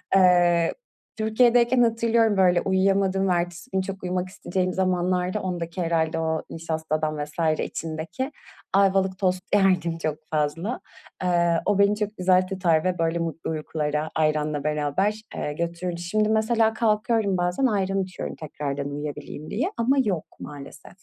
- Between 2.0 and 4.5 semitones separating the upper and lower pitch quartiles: Yes, average, 3.6 semitones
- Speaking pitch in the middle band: Yes, medium, 180 Hz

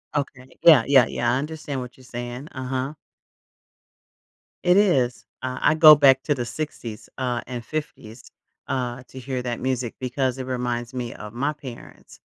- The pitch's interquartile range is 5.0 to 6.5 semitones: No, narrow, 2.4 semitones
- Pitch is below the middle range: Yes, low, 130 Hz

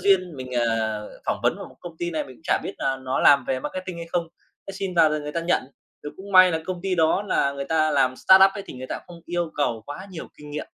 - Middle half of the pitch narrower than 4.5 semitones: No, average, 5.0 semitones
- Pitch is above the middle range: No, medium, 160 Hz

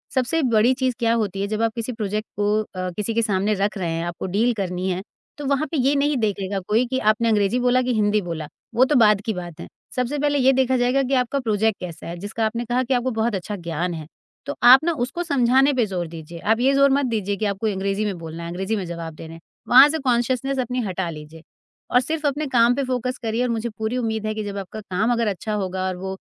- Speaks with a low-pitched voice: No, high, 220 Hz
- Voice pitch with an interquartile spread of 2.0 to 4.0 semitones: No, average, 4.6 semitones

